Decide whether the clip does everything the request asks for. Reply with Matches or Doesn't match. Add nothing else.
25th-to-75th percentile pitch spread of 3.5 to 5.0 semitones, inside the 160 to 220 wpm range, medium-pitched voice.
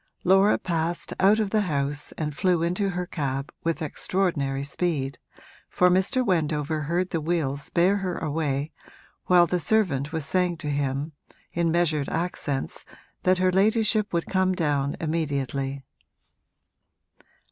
Doesn't match